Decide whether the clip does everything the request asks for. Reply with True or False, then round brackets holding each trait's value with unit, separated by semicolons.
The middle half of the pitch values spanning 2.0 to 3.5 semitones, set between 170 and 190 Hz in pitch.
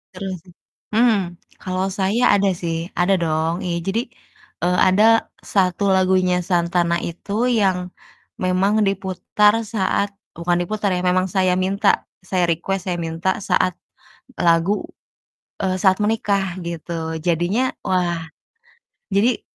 True (2.4 semitones; 185 Hz)